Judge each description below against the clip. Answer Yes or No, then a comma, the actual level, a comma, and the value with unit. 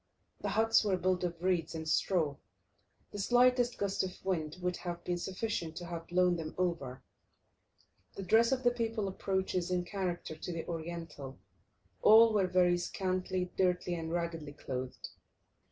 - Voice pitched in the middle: Yes, medium, 180 Hz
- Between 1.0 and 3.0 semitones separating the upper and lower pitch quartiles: Yes, narrow, 2.4 semitones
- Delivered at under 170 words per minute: Yes, average, 155 wpm